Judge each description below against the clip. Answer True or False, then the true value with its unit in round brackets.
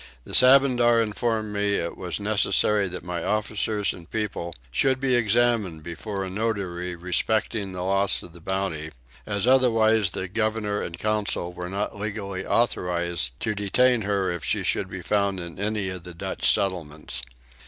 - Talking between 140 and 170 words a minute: True (165 wpm)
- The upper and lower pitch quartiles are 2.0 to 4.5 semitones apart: True (3.5 semitones)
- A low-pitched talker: True (100 Hz)